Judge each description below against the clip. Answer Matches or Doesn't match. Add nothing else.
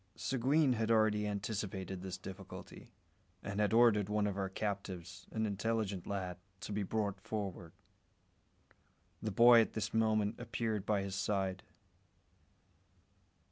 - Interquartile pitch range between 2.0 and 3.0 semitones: Matches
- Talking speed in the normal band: Doesn't match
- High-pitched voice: Doesn't match